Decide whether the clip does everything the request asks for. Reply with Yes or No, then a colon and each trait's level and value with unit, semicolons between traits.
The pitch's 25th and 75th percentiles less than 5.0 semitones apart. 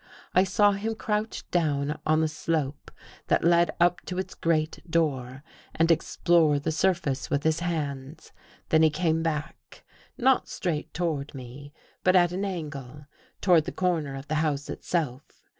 Yes: average, 3.3 semitones